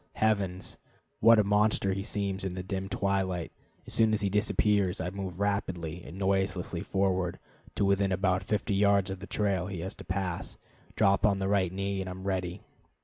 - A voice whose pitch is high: No, very low, 95 Hz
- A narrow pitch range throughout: Yes, narrow, 1.4 semitones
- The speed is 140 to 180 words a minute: No, average, 190 wpm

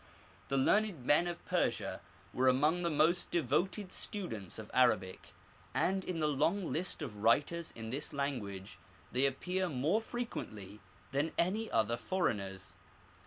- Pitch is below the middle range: No, medium, 145 Hz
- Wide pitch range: Yes, wide, 7.6 semitones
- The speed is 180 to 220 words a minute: No, average, 140 wpm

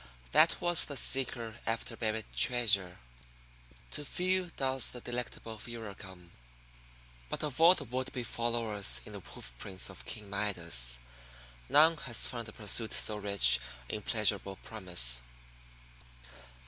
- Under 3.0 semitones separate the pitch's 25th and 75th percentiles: No, average, 4.1 semitones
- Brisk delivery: No, slow, 135 wpm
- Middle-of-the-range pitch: No, low, 110 Hz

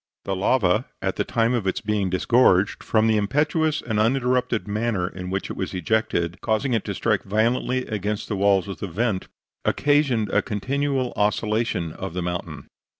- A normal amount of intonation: Yes, average, 4.1 semitones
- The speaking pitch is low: Yes, low, 105 Hz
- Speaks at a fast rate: No, average, 175 wpm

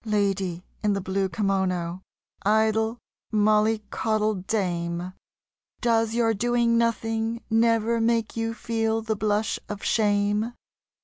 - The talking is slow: Yes, slow, 110 wpm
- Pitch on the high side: Yes, high, 215 Hz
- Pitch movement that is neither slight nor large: No, narrow, 2.3 semitones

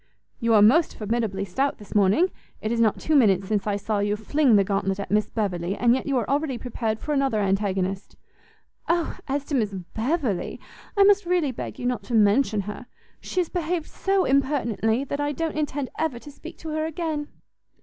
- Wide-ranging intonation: Yes, wide, 6.2 semitones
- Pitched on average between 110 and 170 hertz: No, high, 240 Hz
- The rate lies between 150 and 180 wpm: No, average, 200 wpm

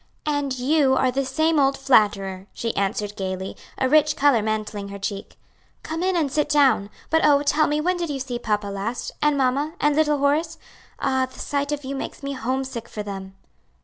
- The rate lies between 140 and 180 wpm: No, average, 200 wpm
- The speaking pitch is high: Yes, very high, 270 Hz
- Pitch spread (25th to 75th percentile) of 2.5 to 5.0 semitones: No, wide, 5.5 semitones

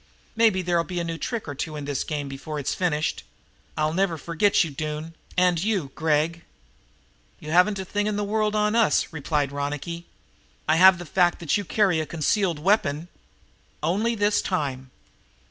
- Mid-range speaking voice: Yes, medium, 170 Hz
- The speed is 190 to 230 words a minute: No, average, 175 wpm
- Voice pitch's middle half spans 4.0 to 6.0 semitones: Yes, average, 4.6 semitones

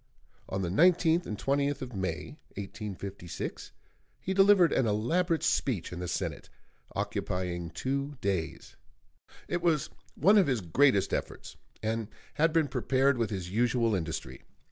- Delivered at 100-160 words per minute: Yes, average, 140 wpm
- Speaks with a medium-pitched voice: No, low, 120 Hz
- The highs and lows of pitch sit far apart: Yes, wide, 8.2 semitones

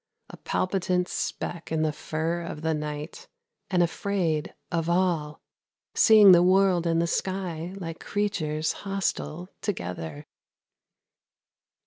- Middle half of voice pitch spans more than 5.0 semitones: No, average, 3.1 semitones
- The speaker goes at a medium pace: No, slow, 115 wpm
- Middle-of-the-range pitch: Yes, medium, 170 Hz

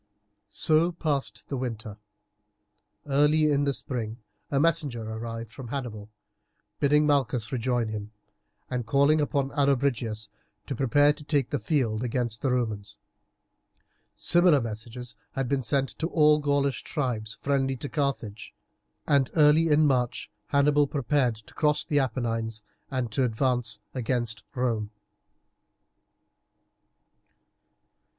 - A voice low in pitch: Yes, low, 130 Hz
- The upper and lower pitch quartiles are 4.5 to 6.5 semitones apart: No, average, 4.0 semitones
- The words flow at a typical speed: No, slow, 125 wpm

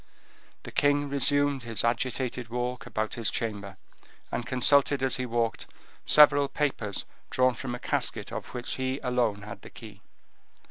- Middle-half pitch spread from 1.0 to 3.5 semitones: Yes, average, 2.9 semitones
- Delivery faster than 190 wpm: No, average, 150 wpm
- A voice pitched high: No, low, 125 Hz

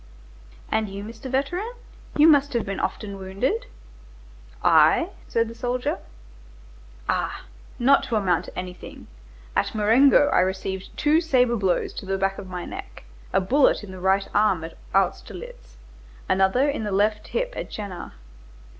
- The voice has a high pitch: Yes, high, 210 Hz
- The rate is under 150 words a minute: No, average, 155 wpm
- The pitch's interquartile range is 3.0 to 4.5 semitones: No, wide, 5.4 semitones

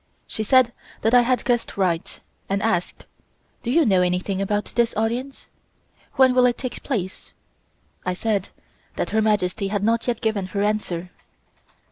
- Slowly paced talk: No, average, 160 wpm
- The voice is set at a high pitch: Yes, high, 215 Hz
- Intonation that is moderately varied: Yes, average, 3.8 semitones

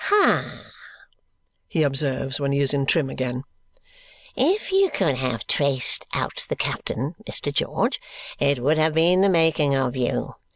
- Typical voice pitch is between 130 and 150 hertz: Yes, medium, 140 Hz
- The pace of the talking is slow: No, average, 155 wpm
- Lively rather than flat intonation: No, average, 3.4 semitones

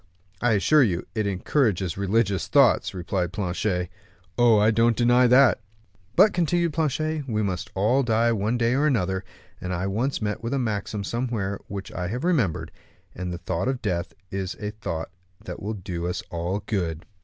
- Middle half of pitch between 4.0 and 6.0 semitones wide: Yes, average, 4.6 semitones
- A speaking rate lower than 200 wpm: Yes, average, 180 wpm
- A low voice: Yes, low, 105 Hz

